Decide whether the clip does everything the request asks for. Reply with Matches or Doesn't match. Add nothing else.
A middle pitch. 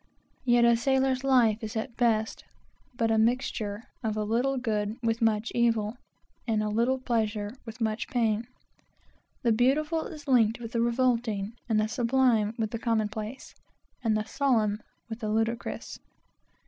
Doesn't match